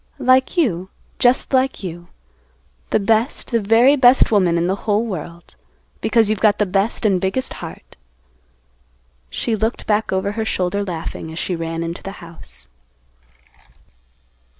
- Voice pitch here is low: No, high, 205 Hz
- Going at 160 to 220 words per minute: No, average, 150 wpm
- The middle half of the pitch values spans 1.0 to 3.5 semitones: No, average, 4.2 semitones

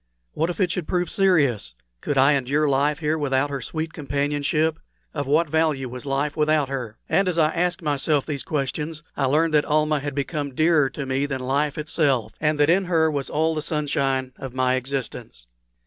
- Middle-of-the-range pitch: Yes, medium, 145 Hz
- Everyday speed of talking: Yes, average, 195 wpm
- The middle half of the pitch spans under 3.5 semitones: Yes, narrow, 2.6 semitones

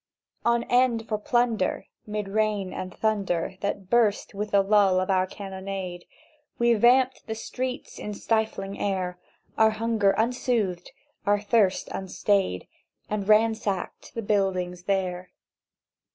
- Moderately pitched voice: No, high, 205 Hz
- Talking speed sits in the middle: No, slow, 130 wpm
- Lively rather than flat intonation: No, average, 2.8 semitones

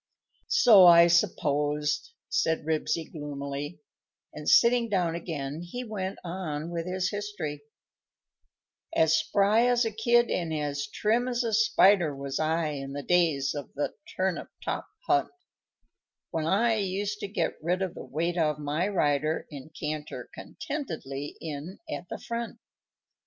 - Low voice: No, medium, 170 Hz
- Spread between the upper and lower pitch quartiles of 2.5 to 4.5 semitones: No, wide, 5.6 semitones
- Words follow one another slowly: No, average, 145 wpm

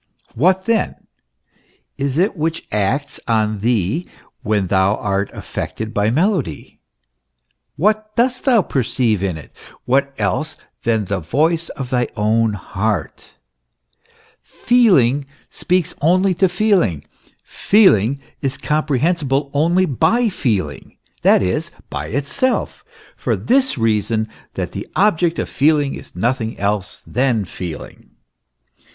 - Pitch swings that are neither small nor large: No, wide, 8.6 semitones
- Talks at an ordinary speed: No, slow, 120 wpm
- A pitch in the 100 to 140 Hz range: Yes, low, 135 Hz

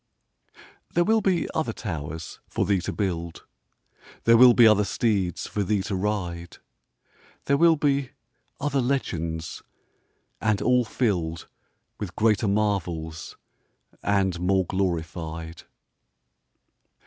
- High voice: No, low, 100 Hz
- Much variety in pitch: Yes, wide, 5.8 semitones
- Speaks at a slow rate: Yes, slow, 115 wpm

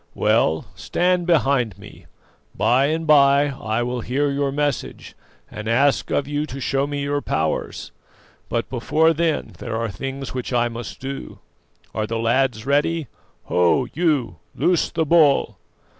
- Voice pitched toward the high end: No, low, 135 Hz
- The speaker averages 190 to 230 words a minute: No, average, 150 wpm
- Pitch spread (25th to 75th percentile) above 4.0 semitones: No, average, 3.7 semitones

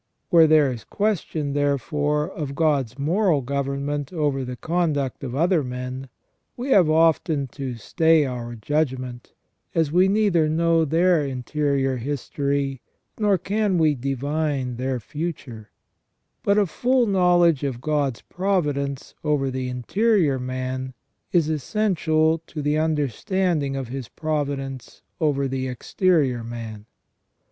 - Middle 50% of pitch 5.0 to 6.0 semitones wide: No, average, 3.9 semitones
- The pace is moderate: No, slow, 130 wpm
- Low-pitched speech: No, medium, 145 Hz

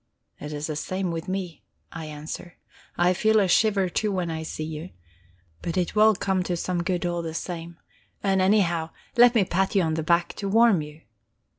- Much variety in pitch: No, average, 3.0 semitones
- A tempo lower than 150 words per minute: No, average, 200 wpm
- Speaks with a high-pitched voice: No, medium, 175 Hz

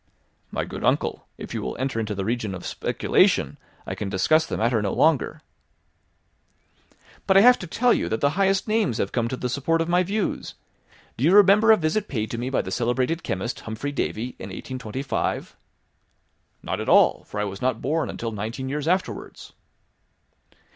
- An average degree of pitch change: No, wide, 7.5 semitones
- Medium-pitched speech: No, low, 130 Hz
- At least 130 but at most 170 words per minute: No, average, 190 wpm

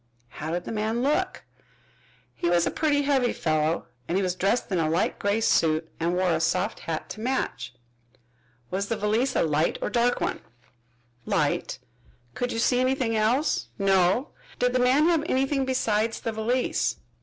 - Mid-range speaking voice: No, high, 220 Hz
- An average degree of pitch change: No, wide, 6.3 semitones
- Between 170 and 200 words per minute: Yes, average, 180 wpm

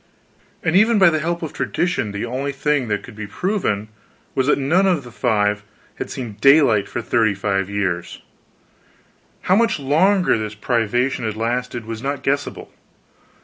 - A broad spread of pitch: Yes, wide, 6.3 semitones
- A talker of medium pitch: No, low, 125 Hz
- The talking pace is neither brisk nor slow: Yes, average, 165 wpm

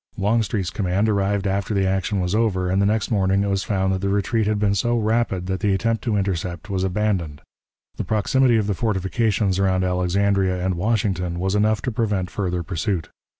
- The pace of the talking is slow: No, average, 195 wpm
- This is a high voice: No, low, 100 Hz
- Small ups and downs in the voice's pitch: Yes, narrow, 2.3 semitones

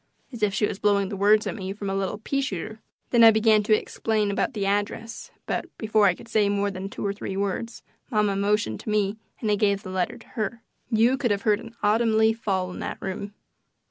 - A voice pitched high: Yes, high, 210 Hz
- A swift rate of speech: Yes, fast, 235 wpm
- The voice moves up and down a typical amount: No, narrow, 1.8 semitones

